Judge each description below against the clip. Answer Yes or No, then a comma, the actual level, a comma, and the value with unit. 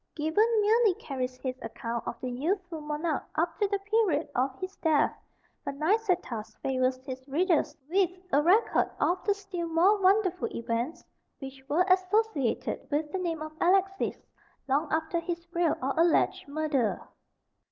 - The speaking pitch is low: No, very high, 330 Hz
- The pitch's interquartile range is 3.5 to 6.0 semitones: Yes, wide, 5.4 semitones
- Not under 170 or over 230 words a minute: No, average, 150 wpm